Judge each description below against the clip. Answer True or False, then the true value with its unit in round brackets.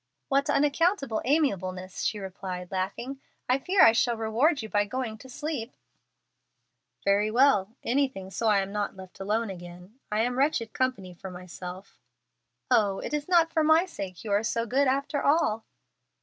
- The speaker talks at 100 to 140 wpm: False (165 wpm)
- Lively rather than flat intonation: True (6.1 semitones)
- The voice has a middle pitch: False (225 Hz)